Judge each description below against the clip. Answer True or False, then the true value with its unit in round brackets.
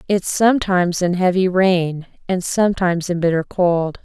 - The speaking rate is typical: True (150 wpm)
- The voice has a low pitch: False (180 Hz)